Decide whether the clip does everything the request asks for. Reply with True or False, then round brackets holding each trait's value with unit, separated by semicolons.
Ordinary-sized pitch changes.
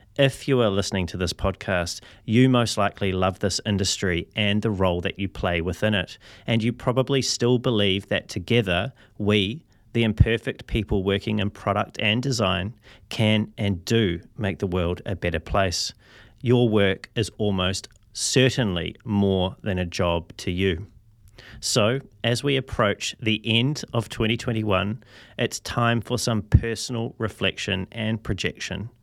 True (3.2 semitones)